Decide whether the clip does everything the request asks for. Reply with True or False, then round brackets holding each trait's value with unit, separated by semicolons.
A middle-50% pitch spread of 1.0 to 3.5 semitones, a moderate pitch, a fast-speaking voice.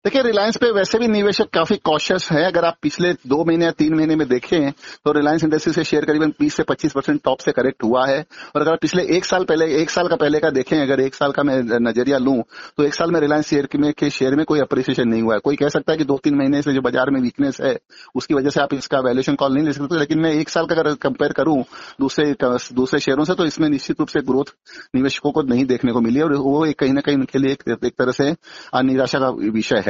True (2.9 semitones; 150 Hz; 265 wpm)